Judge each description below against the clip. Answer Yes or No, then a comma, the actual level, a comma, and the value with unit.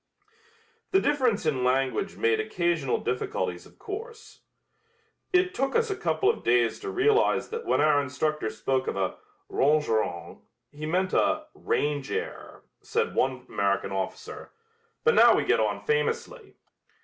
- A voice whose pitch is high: No, medium, 155 Hz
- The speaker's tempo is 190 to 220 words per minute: No, average, 145 wpm